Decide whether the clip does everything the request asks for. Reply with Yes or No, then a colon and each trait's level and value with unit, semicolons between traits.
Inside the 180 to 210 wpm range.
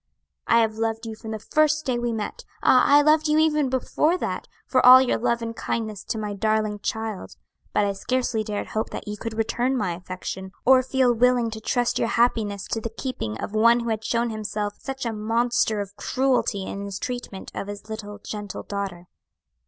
Yes: fast, 205 wpm